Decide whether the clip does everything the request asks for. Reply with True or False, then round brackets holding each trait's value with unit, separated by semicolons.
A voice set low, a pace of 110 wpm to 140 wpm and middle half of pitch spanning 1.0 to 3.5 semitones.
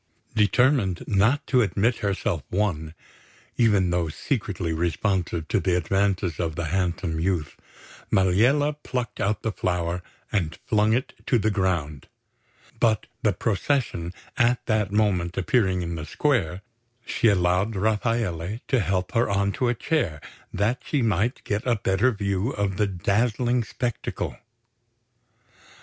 False (100 Hz; 135 wpm; 4.3 semitones)